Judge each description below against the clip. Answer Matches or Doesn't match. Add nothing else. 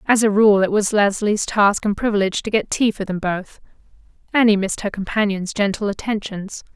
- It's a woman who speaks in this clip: Matches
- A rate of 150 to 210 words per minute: Matches